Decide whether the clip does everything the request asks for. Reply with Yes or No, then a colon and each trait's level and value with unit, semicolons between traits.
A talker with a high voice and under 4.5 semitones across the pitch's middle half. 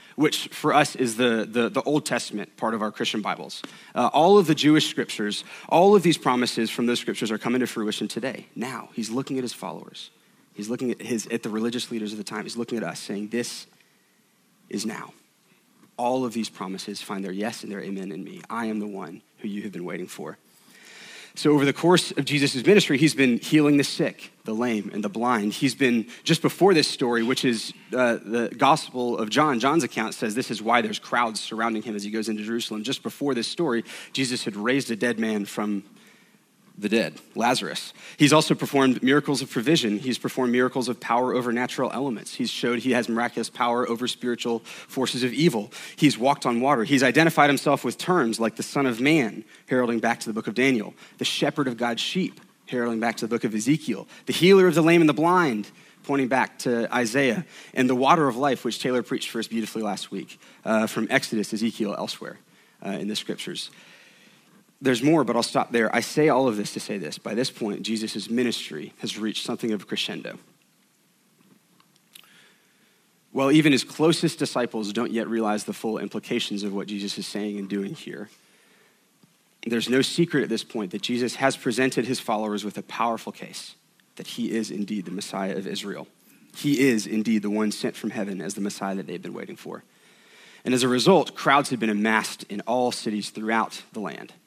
No: low, 120 Hz; average, 4.1 semitones